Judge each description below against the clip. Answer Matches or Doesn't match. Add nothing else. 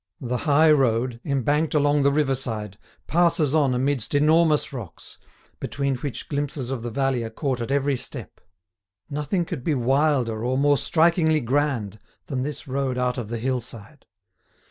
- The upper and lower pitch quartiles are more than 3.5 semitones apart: Doesn't match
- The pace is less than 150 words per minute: Doesn't match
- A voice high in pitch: Doesn't match